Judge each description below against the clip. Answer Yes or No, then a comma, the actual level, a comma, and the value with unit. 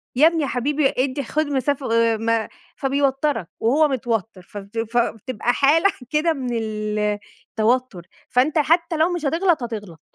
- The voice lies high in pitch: Yes, very high, 255 Hz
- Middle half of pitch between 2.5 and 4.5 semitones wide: No, average, 5.0 semitones